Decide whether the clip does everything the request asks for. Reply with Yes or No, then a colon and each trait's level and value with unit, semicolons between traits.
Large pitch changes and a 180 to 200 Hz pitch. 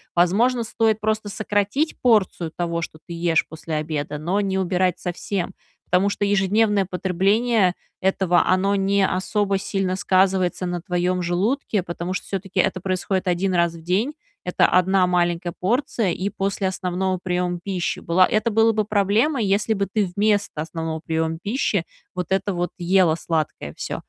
No: narrow, 2.6 semitones; medium, 185 Hz